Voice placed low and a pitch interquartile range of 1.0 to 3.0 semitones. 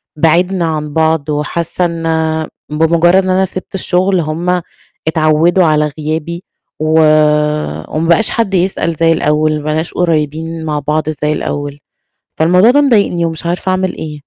No: medium, 165 Hz; narrow, 2.6 semitones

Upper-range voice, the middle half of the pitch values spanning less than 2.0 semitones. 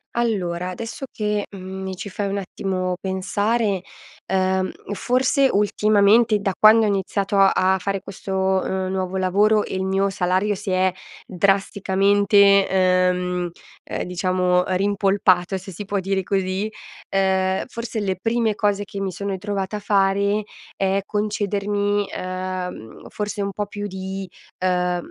Yes: high, 195 Hz; narrow, 1.6 semitones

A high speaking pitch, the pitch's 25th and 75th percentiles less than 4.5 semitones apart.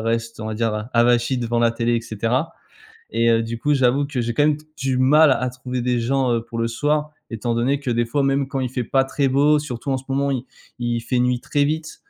No: low, 125 Hz; average, 2.9 semitones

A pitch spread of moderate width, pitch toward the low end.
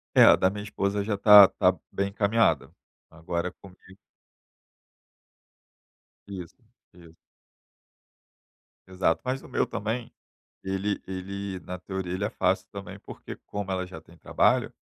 No: narrow, 1.8 semitones; very low, 95 Hz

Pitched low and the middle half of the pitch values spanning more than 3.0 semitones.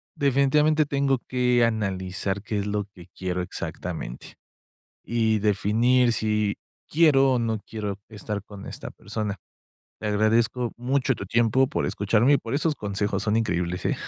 Yes: low, 110 Hz; average, 3.9 semitones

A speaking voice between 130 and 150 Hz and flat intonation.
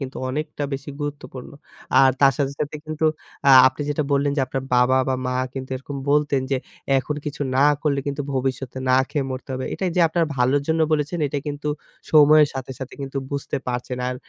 Yes: medium, 140 Hz; narrow, 2.1 semitones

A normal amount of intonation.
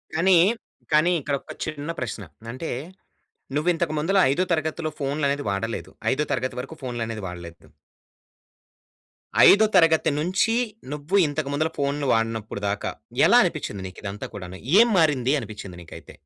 No: wide, 5.9 semitones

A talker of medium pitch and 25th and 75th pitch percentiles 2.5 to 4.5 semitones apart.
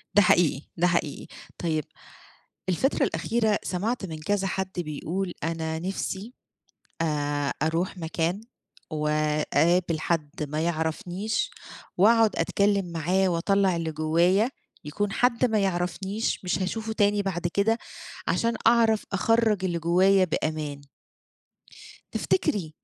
Yes: medium, 180 Hz; average, 4.0 semitones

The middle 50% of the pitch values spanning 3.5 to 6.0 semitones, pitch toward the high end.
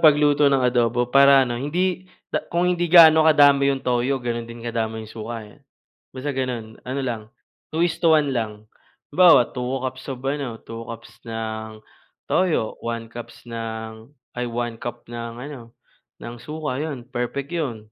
No: average, 3.8 semitones; low, 125 Hz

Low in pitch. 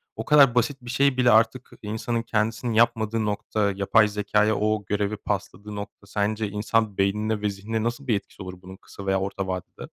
Yes: low, 105 Hz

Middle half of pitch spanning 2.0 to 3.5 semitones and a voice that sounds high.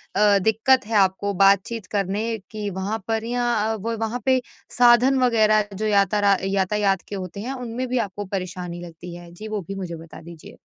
Yes: average, 2.9 semitones; high, 205 Hz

